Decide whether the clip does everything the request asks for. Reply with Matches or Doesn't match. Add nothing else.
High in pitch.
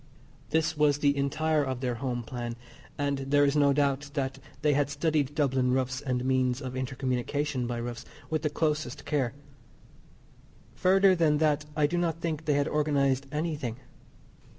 Doesn't match